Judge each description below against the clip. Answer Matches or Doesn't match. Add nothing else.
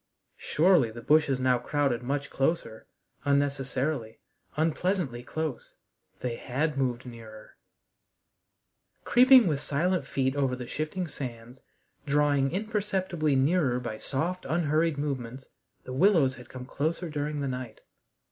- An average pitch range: Matches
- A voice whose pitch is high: Doesn't match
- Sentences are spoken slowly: Matches